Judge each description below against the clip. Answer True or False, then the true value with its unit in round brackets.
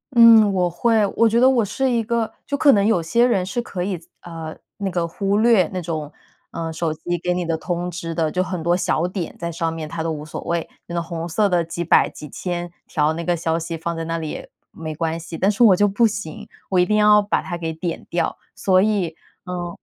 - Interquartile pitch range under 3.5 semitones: False (3.8 semitones)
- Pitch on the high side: False (175 Hz)